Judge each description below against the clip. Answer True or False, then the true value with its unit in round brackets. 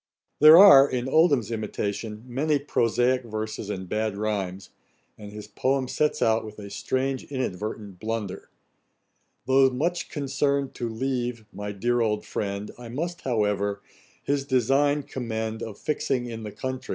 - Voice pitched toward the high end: False (120 Hz)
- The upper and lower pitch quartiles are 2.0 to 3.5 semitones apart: False (4.2 semitones)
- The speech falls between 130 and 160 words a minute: True (145 wpm)